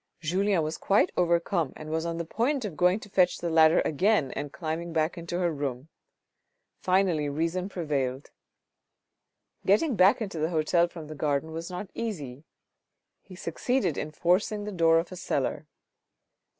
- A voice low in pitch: No, medium, 170 Hz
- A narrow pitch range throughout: No, average, 3.1 semitones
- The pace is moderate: Yes, average, 165 wpm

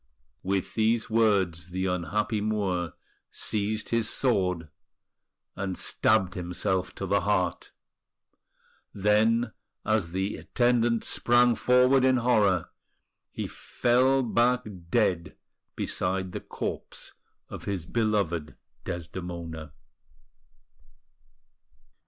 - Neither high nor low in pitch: No, low, 100 Hz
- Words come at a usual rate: No, slow, 90 wpm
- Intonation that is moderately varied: Yes, average, 4.2 semitones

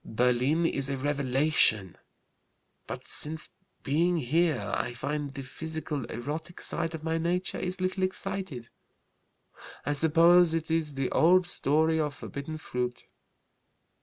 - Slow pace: Yes, slow, 130 wpm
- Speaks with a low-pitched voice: No, medium, 155 Hz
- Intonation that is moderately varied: Yes, average, 3.5 semitones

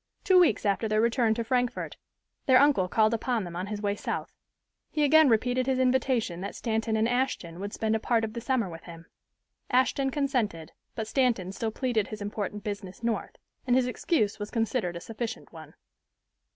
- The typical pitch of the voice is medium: No, high, 225 Hz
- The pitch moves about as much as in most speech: Yes, average, 3.6 semitones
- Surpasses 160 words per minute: Yes, average, 190 wpm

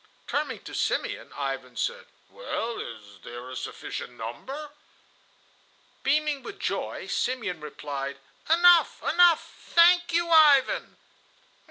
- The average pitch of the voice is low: No, very high, 270 Hz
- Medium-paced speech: No, slow, 110 wpm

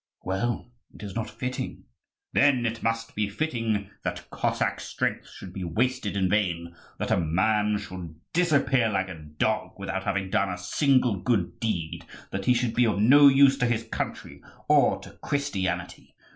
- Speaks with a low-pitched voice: Yes, low, 105 Hz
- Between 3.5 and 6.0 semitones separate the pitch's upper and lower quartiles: Yes, average, 4.8 semitones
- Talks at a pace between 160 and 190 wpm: Yes, average, 170 wpm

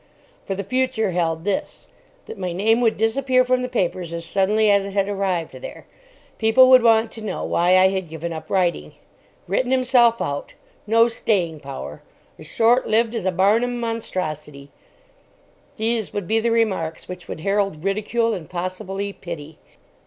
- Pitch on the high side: Yes, high, 200 Hz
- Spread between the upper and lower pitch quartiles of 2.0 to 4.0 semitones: No, average, 4.6 semitones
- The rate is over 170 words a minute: No, average, 165 wpm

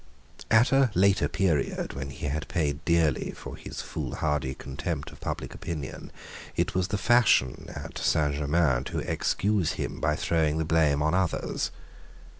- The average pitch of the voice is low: Yes, very low, 80 Hz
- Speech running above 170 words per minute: No, average, 155 wpm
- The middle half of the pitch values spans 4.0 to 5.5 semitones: Yes, average, 4.3 semitones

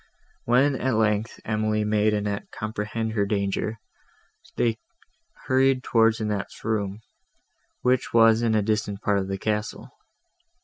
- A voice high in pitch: No, low, 110 Hz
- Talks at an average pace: No, slow, 130 wpm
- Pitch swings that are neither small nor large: No, narrow, 1.5 semitones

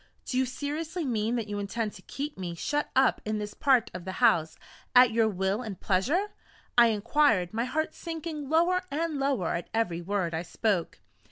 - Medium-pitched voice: No, high, 230 Hz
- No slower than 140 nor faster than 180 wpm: No, average, 190 wpm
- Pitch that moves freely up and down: Yes, wide, 6.6 semitones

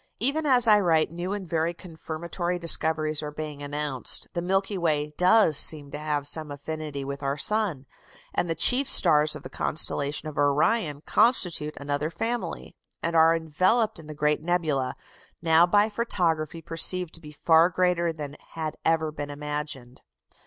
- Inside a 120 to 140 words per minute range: No, average, 165 wpm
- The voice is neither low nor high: Yes, medium, 160 Hz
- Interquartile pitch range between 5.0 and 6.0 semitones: No, average, 3.1 semitones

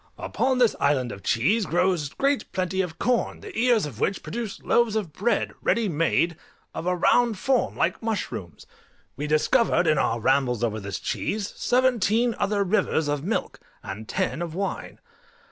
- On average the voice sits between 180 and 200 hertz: Yes, medium, 185 Hz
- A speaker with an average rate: Yes, average, 165 wpm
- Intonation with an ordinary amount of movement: No, wide, 7.3 semitones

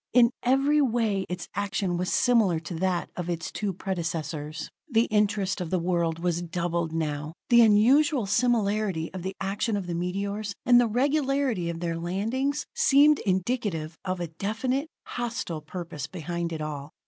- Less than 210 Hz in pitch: Yes, high, 190 Hz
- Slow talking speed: No, average, 160 wpm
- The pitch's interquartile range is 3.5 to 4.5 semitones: No, wide, 5.5 semitones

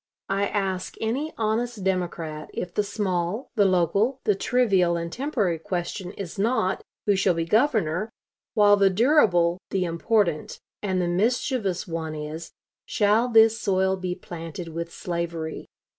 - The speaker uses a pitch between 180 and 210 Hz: Yes, high, 190 Hz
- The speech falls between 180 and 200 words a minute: No, average, 145 wpm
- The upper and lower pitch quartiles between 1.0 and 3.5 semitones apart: No, average, 4.2 semitones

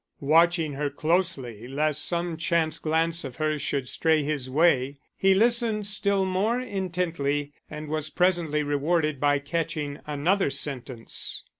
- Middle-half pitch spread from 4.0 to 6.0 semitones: No, average, 3.6 semitones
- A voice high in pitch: No, medium, 155 Hz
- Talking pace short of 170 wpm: Yes, slow, 135 wpm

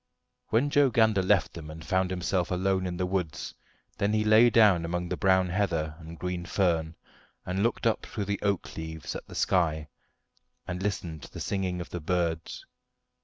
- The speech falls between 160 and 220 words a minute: Yes, average, 185 wpm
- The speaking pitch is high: No, very low, 90 Hz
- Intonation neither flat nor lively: Yes, average, 3.2 semitones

